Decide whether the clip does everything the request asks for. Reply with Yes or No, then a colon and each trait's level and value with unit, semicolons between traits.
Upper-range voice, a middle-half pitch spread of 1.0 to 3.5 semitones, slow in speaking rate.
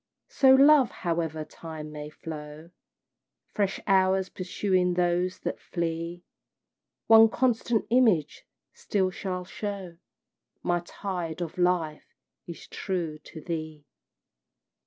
No: medium, 180 Hz; average, 3.2 semitones; slow, 105 wpm